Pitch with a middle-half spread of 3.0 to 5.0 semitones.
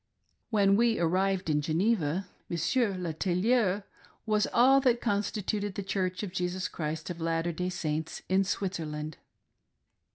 Yes: average, 3.8 semitones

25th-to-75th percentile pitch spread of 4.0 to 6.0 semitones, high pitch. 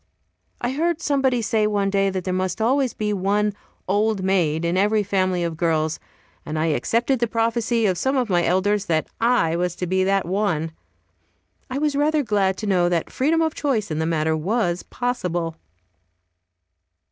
Yes: average, 5.2 semitones; high, 200 Hz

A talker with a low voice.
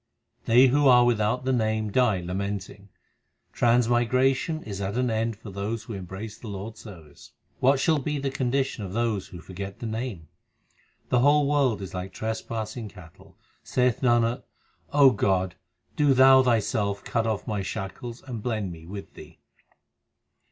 Yes: low, 115 Hz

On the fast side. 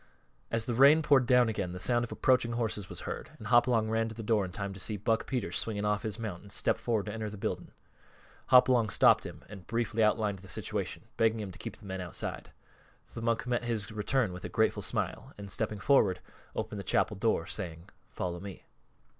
Yes: fast, 220 wpm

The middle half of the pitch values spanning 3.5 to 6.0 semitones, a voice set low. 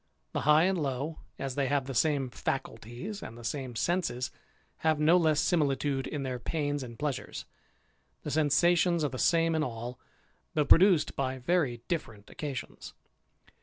No: average, 3.9 semitones; medium, 145 Hz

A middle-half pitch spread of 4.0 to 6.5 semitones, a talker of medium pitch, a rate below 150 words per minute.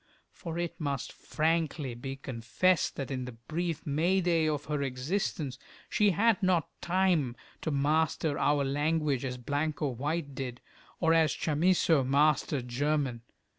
No: average, 3.5 semitones; medium, 150 Hz; average, 140 wpm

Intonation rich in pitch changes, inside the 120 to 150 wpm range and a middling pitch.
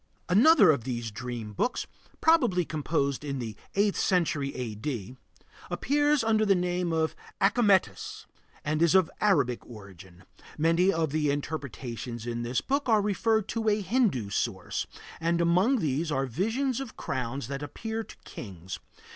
Yes: wide, 8.8 semitones; average, 145 wpm; medium, 160 Hz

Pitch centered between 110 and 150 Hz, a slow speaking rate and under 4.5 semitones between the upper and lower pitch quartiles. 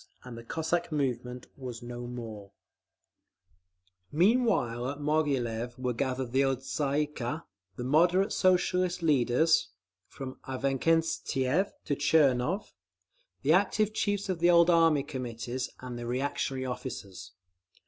No: low, 135 Hz; slow, 120 wpm; average, 4.9 semitones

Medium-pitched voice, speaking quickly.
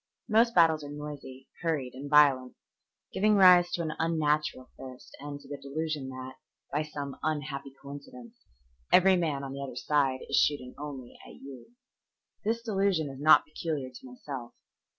No: medium, 145 Hz; average, 160 wpm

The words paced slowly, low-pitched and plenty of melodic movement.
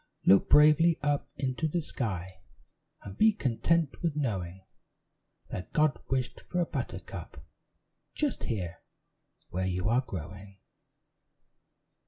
Yes: slow, 115 wpm; low, 125 Hz; wide, 8.3 semitones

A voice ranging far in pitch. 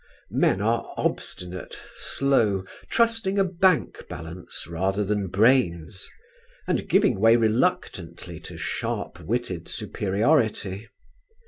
Yes: wide, 6.4 semitones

